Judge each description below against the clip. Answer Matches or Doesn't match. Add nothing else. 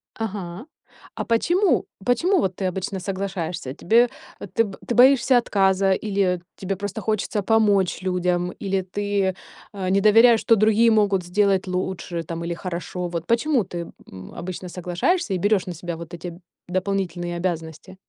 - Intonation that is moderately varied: Matches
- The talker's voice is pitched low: Doesn't match